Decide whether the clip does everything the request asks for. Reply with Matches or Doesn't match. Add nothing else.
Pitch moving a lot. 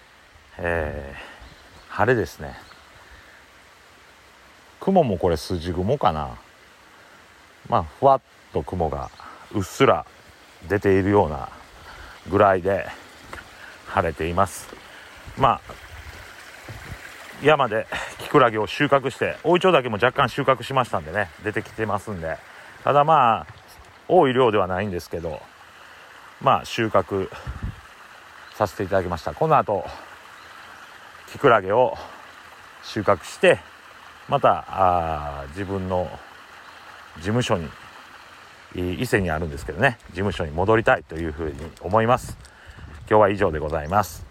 Doesn't match